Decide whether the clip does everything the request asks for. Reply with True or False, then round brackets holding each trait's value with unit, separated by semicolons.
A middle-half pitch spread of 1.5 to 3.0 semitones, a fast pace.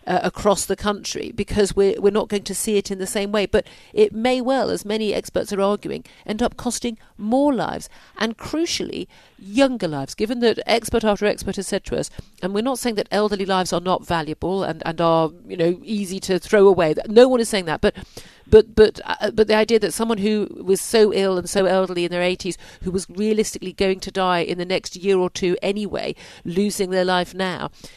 True (2.7 semitones; 220 wpm)